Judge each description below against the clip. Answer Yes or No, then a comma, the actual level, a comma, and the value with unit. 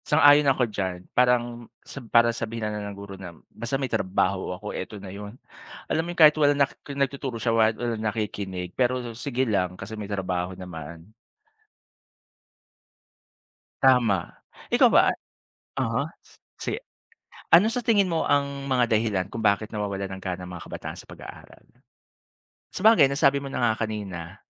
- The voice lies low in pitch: Yes, low, 110 Hz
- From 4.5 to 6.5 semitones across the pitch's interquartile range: Yes, wide, 5.5 semitones